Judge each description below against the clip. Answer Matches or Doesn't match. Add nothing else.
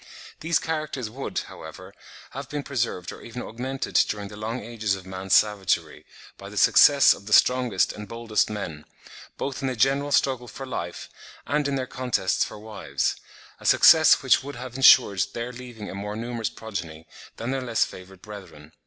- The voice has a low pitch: Matches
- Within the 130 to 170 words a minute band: Doesn't match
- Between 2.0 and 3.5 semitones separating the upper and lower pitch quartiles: Doesn't match